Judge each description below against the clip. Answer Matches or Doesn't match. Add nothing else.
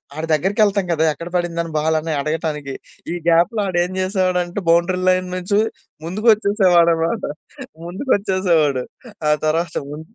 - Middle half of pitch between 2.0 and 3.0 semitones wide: Matches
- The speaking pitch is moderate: Matches